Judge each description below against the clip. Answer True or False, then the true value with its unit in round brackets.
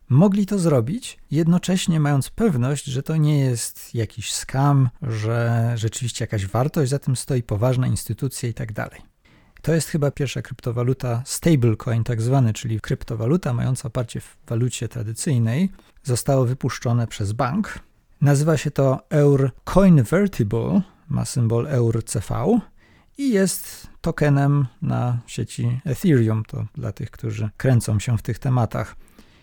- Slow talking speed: False (135 wpm)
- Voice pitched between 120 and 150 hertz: True (130 Hz)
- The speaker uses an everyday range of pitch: True (4.0 semitones)